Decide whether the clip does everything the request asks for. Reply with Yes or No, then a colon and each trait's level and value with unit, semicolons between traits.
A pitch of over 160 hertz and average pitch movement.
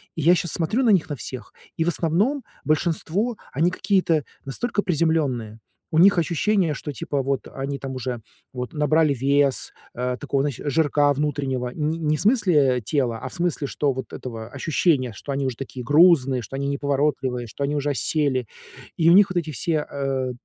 No: medium, 145 Hz; average, 3.9 semitones